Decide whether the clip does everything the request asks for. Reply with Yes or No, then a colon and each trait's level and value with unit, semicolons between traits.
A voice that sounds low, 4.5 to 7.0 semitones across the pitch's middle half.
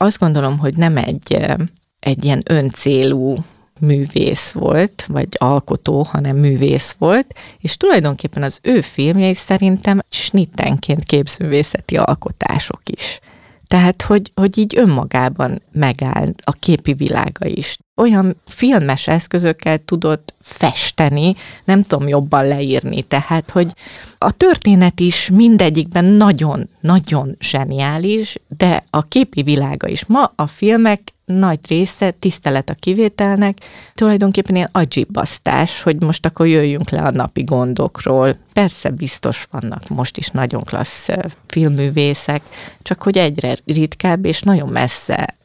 No: medium, 160 Hz; average, 5.0 semitones